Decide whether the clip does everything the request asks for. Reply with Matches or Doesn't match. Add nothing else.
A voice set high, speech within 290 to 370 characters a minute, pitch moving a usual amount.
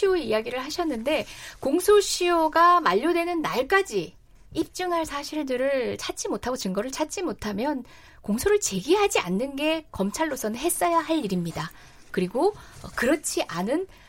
Doesn't match